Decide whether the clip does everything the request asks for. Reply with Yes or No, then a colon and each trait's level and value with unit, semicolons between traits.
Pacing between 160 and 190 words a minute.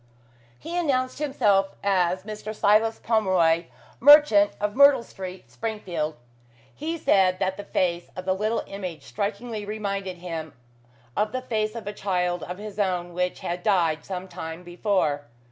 No: average, 150 wpm